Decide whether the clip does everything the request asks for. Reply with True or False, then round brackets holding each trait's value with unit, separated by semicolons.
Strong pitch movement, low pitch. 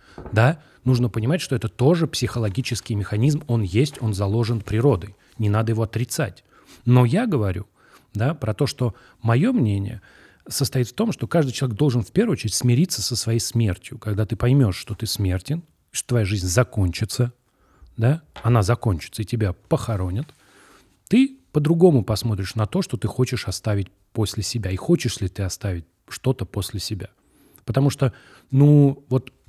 False (3.9 semitones; 115 Hz)